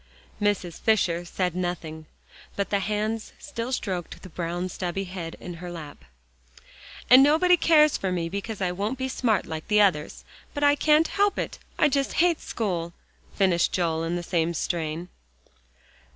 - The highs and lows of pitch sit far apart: Yes, wide, 5.9 semitones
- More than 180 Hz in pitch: Yes, high, 190 Hz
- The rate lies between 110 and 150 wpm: No, average, 165 wpm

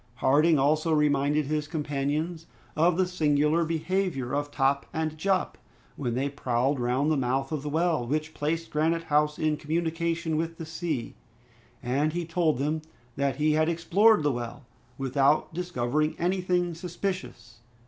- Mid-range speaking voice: Yes, medium, 155 Hz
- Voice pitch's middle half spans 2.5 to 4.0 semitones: Yes, average, 2.9 semitones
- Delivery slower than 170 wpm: Yes, average, 150 wpm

